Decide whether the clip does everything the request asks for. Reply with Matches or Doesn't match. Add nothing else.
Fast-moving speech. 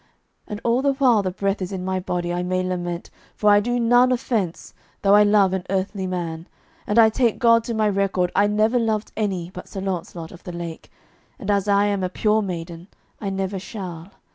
Matches